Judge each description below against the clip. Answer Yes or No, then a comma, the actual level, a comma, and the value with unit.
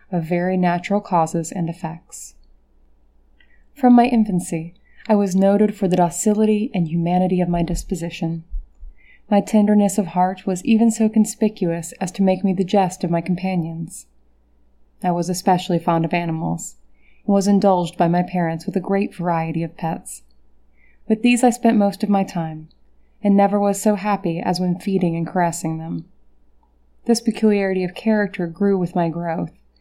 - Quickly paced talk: No, average, 165 wpm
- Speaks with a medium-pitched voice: Yes, medium, 180 Hz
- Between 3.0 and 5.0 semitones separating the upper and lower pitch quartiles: Yes, average, 3.4 semitones